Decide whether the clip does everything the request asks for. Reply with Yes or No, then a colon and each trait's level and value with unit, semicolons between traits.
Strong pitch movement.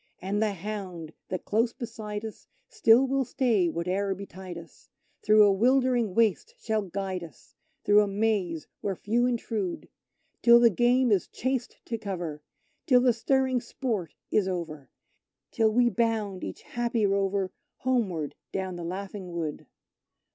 No: average, 4.3 semitones